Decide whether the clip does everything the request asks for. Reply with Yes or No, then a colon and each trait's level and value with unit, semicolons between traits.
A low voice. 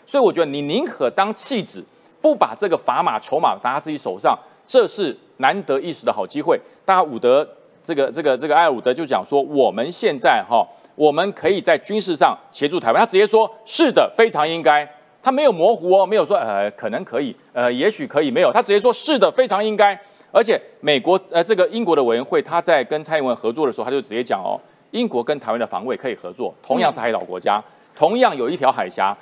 No: high, 195 Hz